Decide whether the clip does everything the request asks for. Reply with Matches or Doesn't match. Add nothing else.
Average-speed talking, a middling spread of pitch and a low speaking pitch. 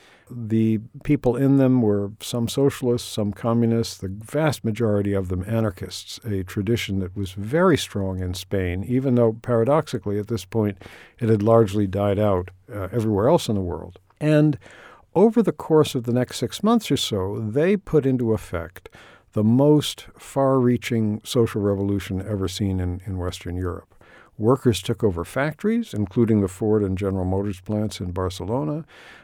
Matches